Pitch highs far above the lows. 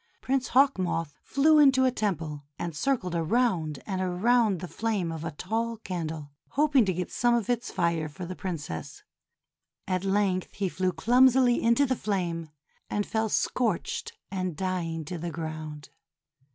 Yes: wide, 6.0 semitones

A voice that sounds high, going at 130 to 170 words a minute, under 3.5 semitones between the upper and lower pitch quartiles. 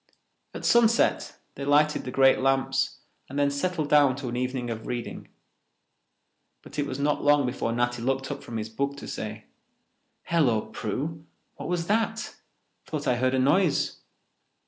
No: low, 135 Hz; average, 165 wpm; average, 3.0 semitones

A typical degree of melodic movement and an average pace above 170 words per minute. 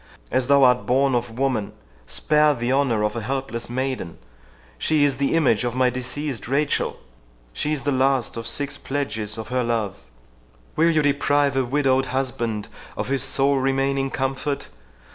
No: average, 3.3 semitones; average, 160 wpm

